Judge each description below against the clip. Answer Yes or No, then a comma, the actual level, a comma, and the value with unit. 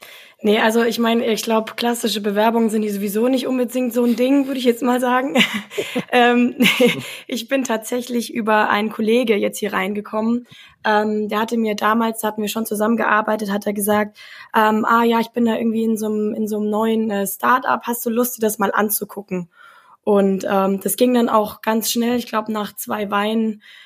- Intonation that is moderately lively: No, narrow, 2.1 semitones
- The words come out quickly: Yes, fast, 195 wpm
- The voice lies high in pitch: Yes, high, 220 Hz